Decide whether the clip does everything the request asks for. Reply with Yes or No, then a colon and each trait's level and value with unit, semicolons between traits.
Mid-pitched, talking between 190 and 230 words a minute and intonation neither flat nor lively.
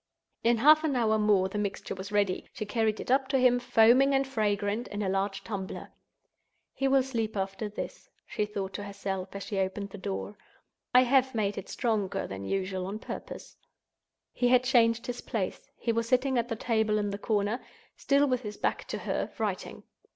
No: high, 215 Hz; average, 195 wpm; average, 3.6 semitones